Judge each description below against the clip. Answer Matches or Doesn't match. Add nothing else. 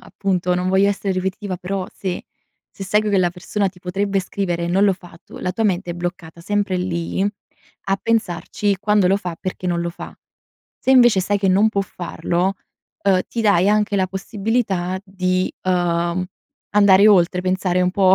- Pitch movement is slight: Matches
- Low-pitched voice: Doesn't match